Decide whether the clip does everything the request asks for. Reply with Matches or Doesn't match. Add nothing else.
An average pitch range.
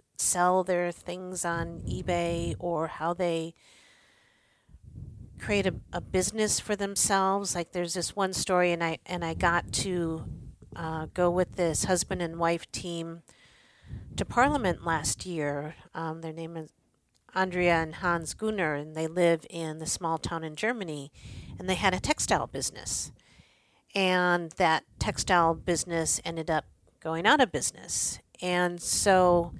Doesn't match